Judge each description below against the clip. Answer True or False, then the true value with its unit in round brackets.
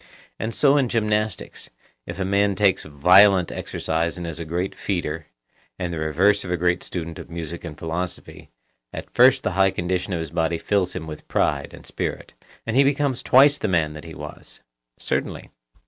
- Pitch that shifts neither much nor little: True (4.0 semitones)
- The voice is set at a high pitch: False (90 Hz)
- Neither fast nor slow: True (190 wpm)